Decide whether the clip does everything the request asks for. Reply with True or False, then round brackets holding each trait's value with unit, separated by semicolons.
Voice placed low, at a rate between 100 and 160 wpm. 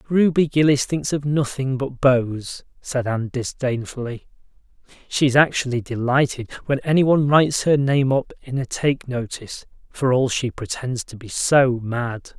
True (130 Hz; 150 wpm)